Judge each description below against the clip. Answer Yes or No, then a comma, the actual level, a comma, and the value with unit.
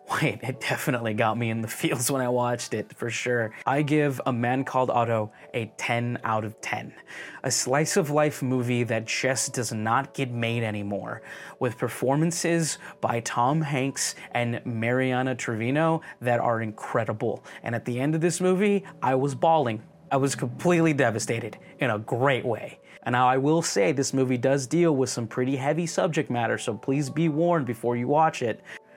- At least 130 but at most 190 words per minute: Yes, average, 180 wpm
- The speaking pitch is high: No, low, 130 Hz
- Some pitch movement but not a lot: Yes, average, 4.0 semitones